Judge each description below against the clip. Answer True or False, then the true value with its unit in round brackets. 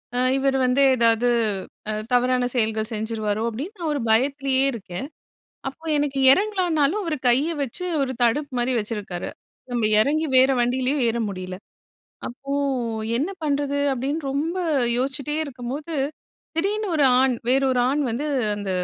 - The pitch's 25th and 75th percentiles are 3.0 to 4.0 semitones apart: True (3.6 semitones)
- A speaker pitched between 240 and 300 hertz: True (265 Hz)